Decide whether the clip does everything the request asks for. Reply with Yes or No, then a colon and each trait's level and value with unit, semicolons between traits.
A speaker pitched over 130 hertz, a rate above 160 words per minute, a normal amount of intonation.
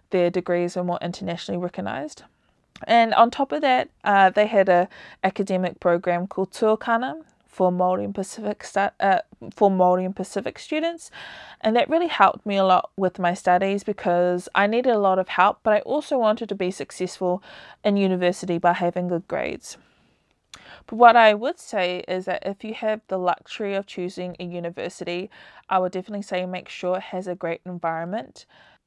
Yes: high, 190 Hz; average, 175 wpm; average, 3.1 semitones